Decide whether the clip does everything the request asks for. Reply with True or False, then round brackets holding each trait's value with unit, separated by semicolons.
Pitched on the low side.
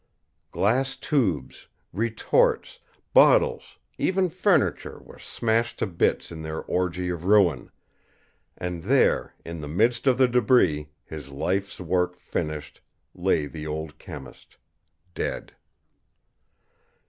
True (90 Hz)